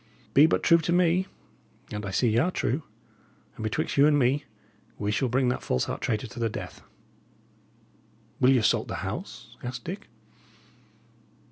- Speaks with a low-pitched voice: Yes, low, 130 Hz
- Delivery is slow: No, average, 170 wpm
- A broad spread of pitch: Yes, wide, 6.1 semitones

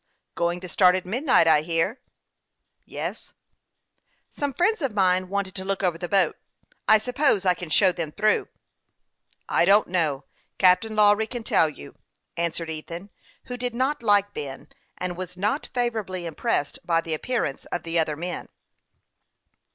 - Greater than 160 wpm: Yes, average, 170 wpm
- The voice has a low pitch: No, medium, 185 Hz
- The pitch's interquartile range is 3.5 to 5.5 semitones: Yes, average, 4.3 semitones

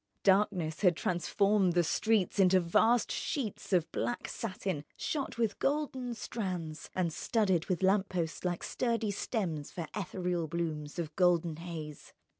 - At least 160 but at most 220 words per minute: No, average, 140 wpm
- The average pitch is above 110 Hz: Yes, medium, 185 Hz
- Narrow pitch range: No, average, 3.9 semitones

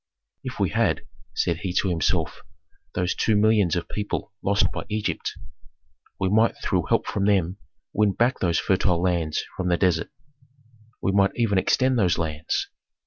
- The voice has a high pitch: No, very low, 95 Hz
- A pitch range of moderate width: Yes, average, 3.0 semitones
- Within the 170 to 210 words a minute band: No, average, 160 wpm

